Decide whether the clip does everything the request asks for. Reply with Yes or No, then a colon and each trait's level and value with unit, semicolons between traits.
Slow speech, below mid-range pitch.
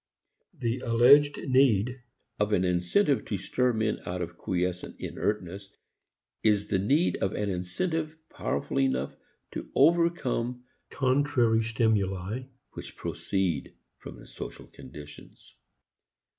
Yes: slow, 115 wpm; low, 110 Hz